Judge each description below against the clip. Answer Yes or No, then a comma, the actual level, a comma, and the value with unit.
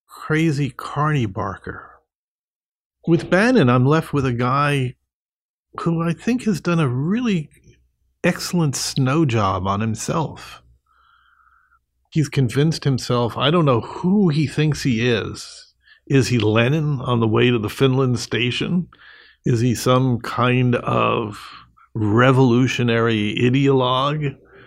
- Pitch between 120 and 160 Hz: Yes, low, 135 Hz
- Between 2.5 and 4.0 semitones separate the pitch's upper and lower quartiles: No, average, 5.2 semitones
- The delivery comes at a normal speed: No, slow, 120 wpm